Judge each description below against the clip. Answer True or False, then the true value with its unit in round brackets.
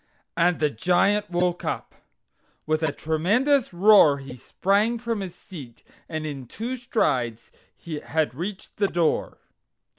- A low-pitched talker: False (175 Hz)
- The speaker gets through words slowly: True (130 wpm)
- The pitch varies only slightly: False (5.5 semitones)